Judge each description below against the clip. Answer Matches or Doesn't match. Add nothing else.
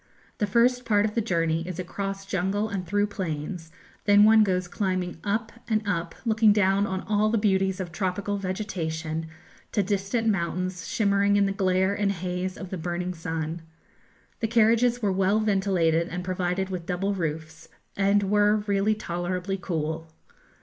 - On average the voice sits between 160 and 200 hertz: Matches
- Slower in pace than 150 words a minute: Doesn't match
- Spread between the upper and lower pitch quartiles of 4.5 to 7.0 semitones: Doesn't match